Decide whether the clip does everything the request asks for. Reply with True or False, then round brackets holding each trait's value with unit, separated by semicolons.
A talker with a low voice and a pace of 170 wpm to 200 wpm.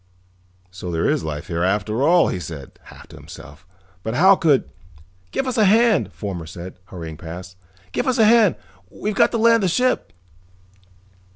True (100 Hz; 180 wpm)